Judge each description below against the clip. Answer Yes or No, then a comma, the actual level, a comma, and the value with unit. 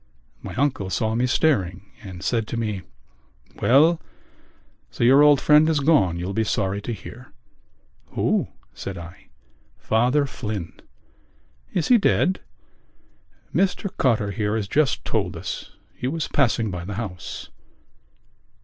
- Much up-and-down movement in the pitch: Yes, wide, 6.6 semitones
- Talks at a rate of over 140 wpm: No, slow, 135 wpm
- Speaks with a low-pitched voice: Yes, low, 115 Hz